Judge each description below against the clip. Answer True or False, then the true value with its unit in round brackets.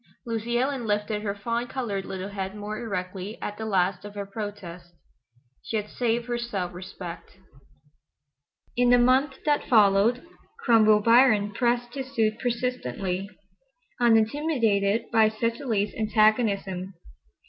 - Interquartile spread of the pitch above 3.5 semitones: False (3.1 semitones)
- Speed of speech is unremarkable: False (125 wpm)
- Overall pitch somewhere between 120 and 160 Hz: False (215 Hz)